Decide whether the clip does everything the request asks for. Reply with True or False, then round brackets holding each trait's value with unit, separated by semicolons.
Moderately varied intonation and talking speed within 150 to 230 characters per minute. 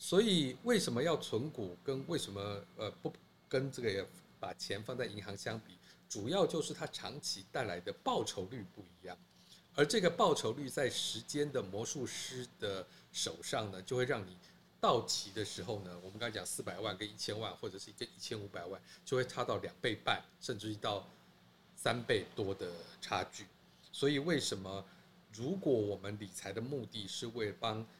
False (4.3 semitones; 265 characters per minute)